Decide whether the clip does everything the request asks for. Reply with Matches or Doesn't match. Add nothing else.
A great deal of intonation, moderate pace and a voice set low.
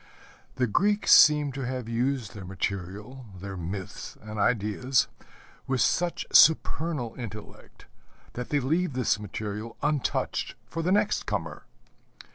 Doesn't match